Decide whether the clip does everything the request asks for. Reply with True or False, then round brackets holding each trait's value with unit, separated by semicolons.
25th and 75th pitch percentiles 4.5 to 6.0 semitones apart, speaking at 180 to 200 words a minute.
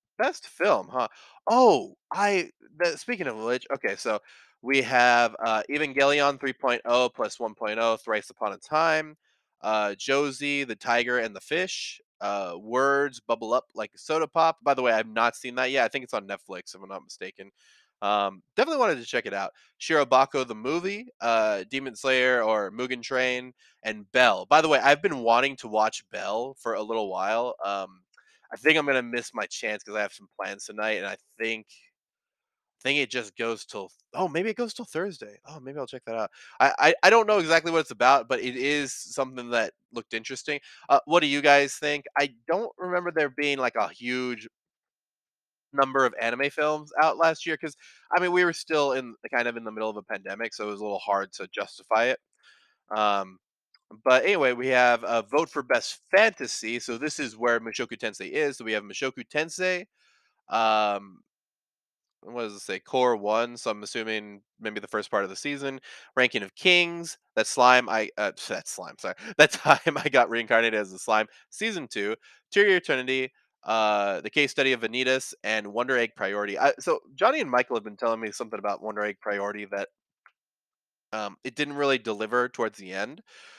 True (4.9 semitones; 195 wpm)